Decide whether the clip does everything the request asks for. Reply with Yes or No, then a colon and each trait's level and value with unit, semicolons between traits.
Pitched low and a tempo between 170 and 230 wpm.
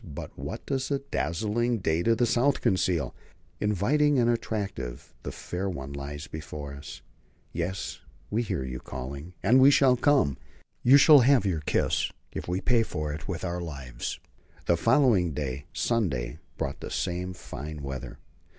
No: very low, 90 Hz; average, 160 wpm